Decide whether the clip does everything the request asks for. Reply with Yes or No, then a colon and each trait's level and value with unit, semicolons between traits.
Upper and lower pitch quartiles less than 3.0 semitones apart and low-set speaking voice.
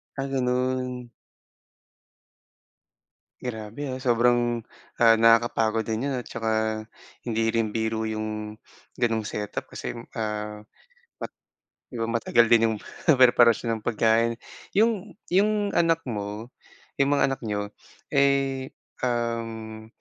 Yes: narrow, 2.6 semitones; low, 115 Hz